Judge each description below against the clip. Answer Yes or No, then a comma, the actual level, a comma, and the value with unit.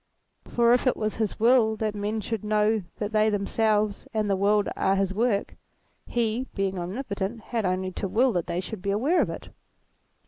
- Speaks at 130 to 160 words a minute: No, average, 195 wpm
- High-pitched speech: Yes, high, 215 Hz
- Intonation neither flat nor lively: No, narrow, 2.3 semitones